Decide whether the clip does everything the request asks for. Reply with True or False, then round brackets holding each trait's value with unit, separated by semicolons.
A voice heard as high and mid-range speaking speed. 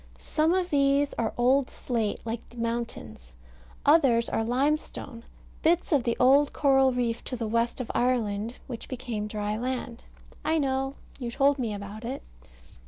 True (245 Hz; 160 wpm)